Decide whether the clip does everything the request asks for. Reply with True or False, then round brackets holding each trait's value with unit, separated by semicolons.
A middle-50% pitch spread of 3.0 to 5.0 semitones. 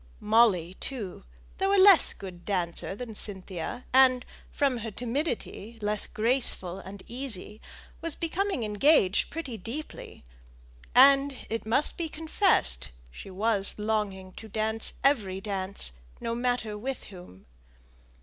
False (5.4 semitones)